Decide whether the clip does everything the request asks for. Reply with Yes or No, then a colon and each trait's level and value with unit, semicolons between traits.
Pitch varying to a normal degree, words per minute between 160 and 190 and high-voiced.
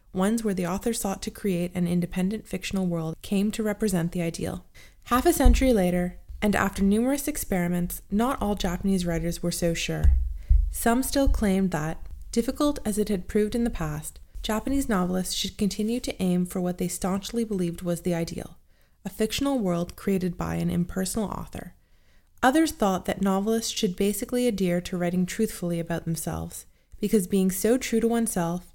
Yes: average, 4.0 semitones; average, 175 wpm; high, 195 Hz